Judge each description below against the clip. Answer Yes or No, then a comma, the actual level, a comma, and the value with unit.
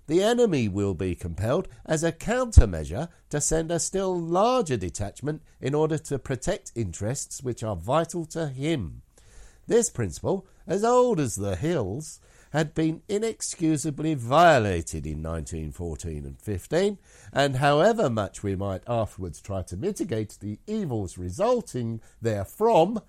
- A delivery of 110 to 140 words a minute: Yes, slow, 135 wpm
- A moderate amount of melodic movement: No, wide, 8.8 semitones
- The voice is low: Yes, low, 130 Hz